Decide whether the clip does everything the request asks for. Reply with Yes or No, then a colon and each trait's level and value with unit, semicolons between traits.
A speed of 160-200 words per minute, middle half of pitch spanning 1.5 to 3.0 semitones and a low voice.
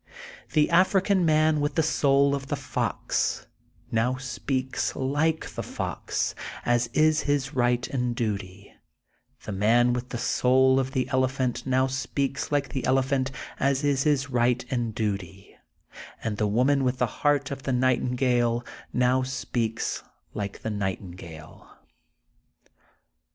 No: average, 140 wpm; narrow, 2.6 semitones; low, 130 Hz